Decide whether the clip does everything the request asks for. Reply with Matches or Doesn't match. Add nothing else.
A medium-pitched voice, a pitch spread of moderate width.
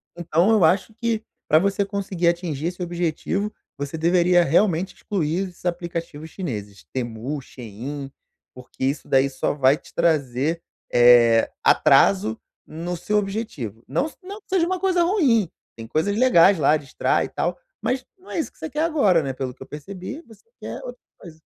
Doesn't match